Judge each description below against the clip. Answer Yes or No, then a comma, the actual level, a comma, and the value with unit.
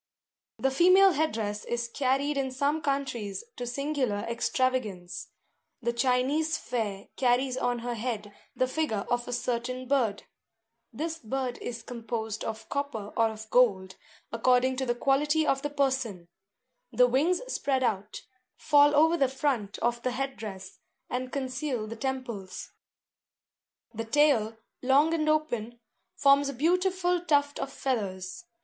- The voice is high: Yes, very high, 255 Hz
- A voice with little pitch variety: No, average, 3.9 semitones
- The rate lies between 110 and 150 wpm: Yes, average, 140 wpm